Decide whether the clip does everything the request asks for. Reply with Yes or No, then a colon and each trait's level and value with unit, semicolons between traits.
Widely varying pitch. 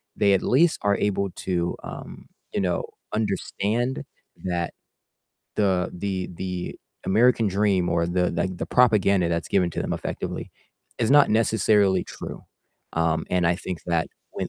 No: average, 3.2 semitones